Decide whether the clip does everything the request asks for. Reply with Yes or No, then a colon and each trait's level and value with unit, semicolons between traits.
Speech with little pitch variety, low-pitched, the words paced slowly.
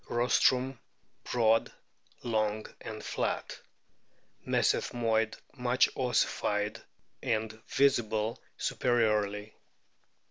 Yes: narrow, 2.2 semitones; low, 110 Hz; slow, 65 wpm